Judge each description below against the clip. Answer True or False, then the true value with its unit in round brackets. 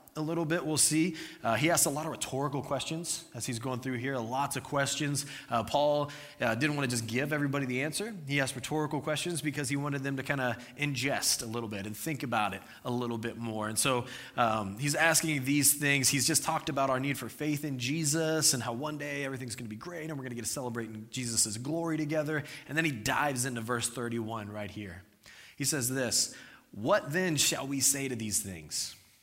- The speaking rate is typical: False (230 wpm)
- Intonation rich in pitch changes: False (3.8 semitones)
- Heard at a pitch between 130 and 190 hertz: True (140 Hz)